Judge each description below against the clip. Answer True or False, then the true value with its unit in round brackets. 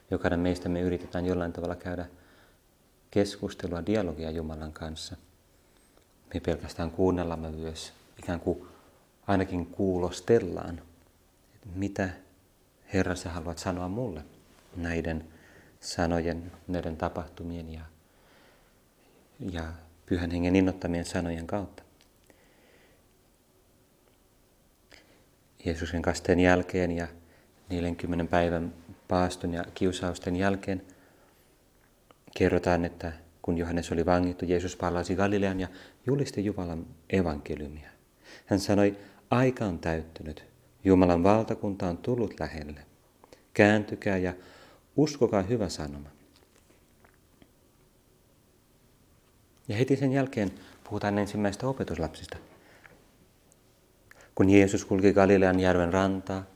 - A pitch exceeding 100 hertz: False (90 Hz)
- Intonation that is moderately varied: False (2.3 semitones)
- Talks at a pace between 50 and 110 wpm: True (95 wpm)